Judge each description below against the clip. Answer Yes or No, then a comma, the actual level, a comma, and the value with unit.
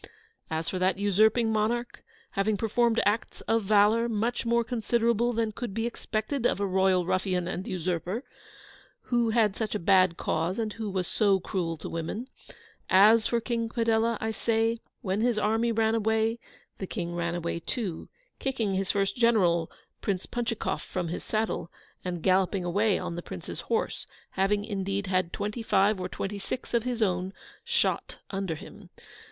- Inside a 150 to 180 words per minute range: Yes, average, 170 wpm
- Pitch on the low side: No, high, 210 Hz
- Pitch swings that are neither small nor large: Yes, average, 3.5 semitones